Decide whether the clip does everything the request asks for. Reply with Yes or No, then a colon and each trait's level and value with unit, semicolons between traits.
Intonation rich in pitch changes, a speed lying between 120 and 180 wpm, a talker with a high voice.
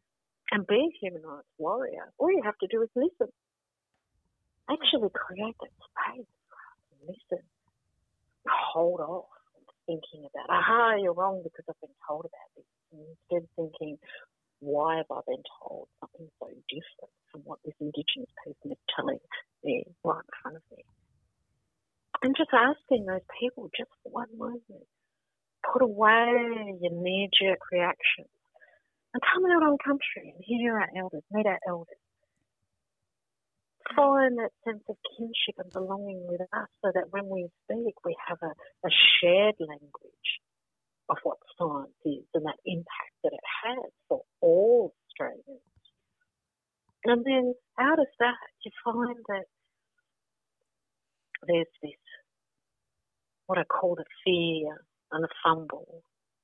Yes: wide, 7.3 semitones; average, 140 wpm; high, 210 Hz